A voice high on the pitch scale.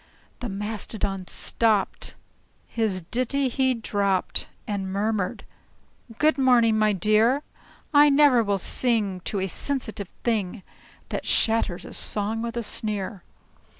Yes: high, 220 Hz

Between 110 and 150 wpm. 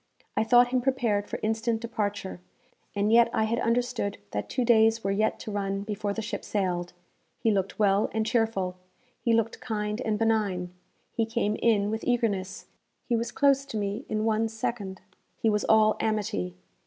No: average, 180 wpm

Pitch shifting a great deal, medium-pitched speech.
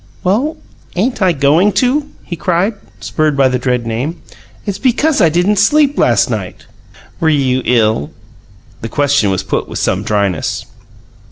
Yes: wide, 8.7 semitones; medium, 160 Hz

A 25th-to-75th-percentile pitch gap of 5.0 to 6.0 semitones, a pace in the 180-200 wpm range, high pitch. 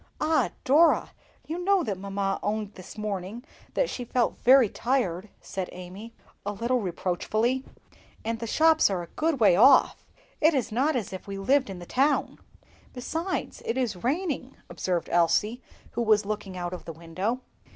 No: wide, 5.5 semitones; average, 170 wpm; high, 225 Hz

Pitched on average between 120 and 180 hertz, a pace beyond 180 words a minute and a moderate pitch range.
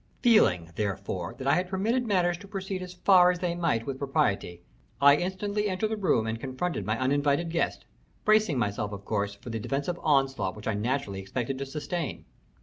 No: medium, 140 Hz; average, 190 wpm; wide, 8.6 semitones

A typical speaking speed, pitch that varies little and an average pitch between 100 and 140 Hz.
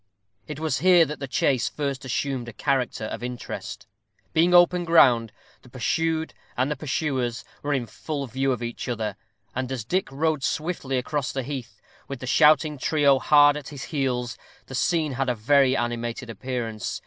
No: average, 170 wpm; average, 3.6 semitones; low, 135 Hz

